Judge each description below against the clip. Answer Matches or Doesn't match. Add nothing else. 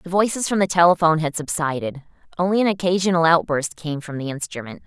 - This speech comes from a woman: Matches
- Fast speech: Doesn't match